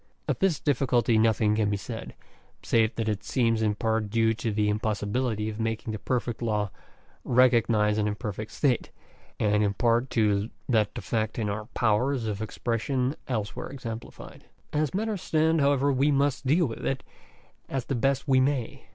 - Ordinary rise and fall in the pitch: Yes, average, 3.6 semitones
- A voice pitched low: Yes, low, 115 Hz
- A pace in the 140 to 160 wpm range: No, average, 175 wpm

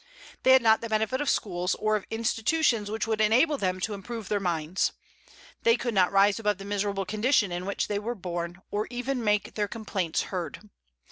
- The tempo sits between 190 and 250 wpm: Yes, average, 200 wpm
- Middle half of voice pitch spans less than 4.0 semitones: Yes, average, 2.8 semitones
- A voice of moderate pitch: No, high, 210 Hz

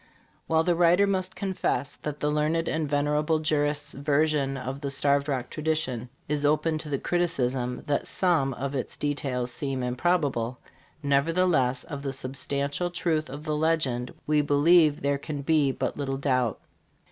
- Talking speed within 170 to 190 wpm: No, average, 160 wpm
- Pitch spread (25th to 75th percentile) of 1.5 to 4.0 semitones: Yes, average, 2.7 semitones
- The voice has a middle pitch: Yes, medium, 145 Hz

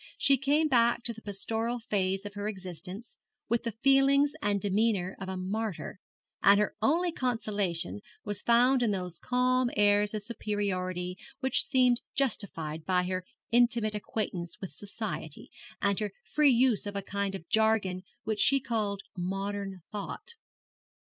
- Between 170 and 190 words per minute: No, average, 150 wpm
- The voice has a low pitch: No, high, 210 Hz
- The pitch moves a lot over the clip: No, average, 3.8 semitones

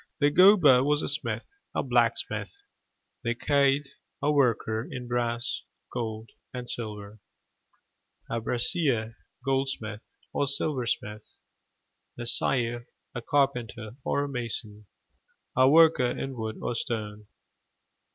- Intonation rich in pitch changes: No, average, 3.7 semitones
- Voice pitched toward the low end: Yes, low, 120 Hz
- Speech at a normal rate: No, slow, 110 wpm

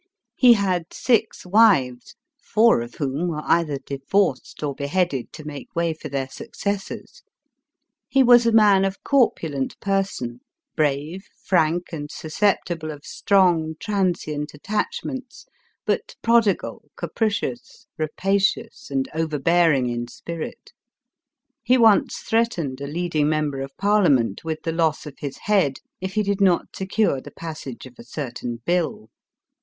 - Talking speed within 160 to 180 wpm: No, average, 140 wpm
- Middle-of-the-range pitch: Yes, medium, 165 Hz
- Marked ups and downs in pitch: Yes, wide, 5.9 semitones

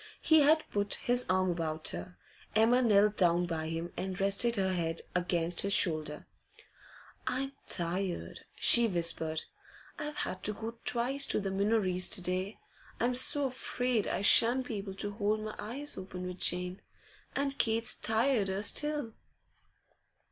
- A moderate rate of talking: Yes, average, 150 wpm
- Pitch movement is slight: No, average, 4.8 semitones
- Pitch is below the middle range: No, high, 200 Hz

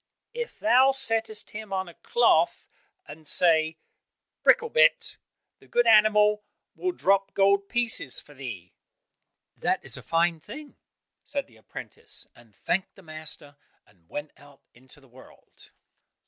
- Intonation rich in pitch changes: Yes, wide, 7.4 semitones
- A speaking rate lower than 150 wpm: Yes, slow, 135 wpm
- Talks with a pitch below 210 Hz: Yes, high, 190 Hz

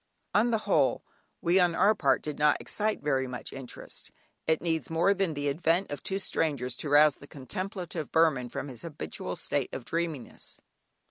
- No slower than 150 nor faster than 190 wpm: Yes, average, 180 wpm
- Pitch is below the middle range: No, medium, 160 Hz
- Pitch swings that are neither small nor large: Yes, average, 4.2 semitones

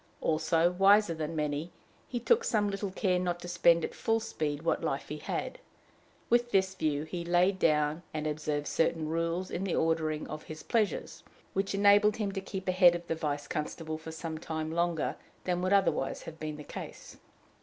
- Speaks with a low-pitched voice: No, medium, 170 Hz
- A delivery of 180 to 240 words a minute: Yes, average, 190 wpm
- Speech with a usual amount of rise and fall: Yes, average, 3.6 semitones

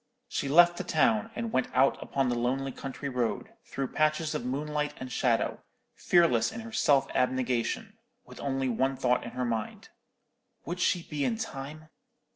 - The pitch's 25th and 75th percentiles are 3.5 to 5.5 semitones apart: Yes, average, 4.1 semitones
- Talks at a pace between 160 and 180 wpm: Yes, average, 170 wpm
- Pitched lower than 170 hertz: Yes, low, 135 Hz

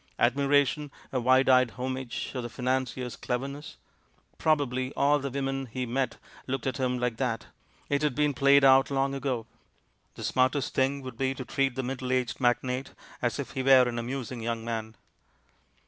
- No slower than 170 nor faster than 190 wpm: Yes, average, 180 wpm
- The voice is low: Yes, low, 130 Hz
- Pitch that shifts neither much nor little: No, narrow, 1.7 semitones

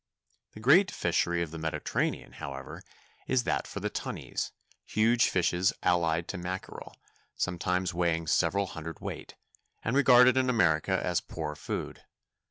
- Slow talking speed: Yes, slow, 125 wpm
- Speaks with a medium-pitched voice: No, very low, 90 Hz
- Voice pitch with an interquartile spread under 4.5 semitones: No, wide, 5.4 semitones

